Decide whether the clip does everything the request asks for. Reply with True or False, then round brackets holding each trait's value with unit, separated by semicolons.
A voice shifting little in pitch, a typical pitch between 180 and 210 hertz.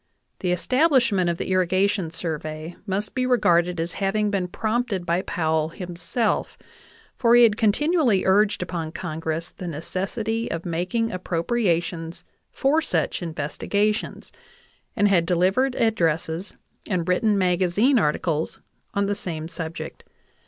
False (4.3 semitones; 185 Hz)